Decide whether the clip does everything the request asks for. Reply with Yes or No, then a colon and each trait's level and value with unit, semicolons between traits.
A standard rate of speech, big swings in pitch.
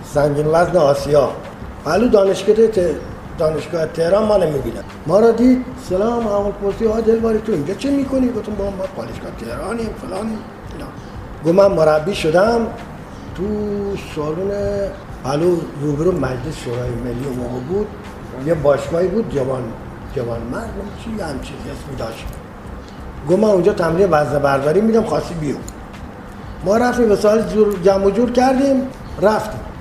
Yes: average, 145 wpm; wide, 6.6 semitones